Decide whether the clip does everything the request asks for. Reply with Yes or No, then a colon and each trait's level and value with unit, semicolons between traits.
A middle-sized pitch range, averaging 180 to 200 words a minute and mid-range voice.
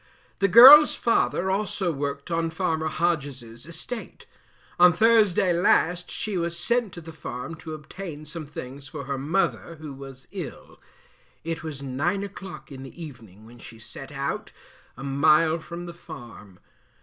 No: average, 4.4 semitones; average, 155 wpm; medium, 160 Hz